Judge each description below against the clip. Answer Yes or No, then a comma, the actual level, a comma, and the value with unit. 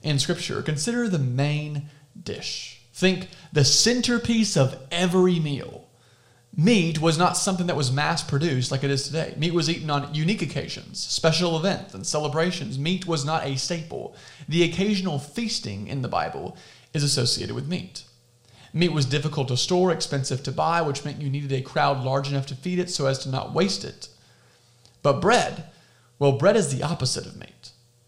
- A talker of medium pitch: Yes, medium, 150 Hz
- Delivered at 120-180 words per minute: Yes, average, 175 wpm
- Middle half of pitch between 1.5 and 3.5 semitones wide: No, average, 4.5 semitones